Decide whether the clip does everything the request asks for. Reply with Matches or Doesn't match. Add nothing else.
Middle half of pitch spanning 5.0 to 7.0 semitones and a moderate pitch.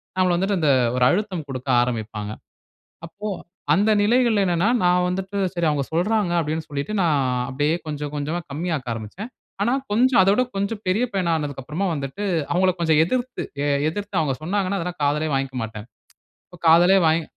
Matches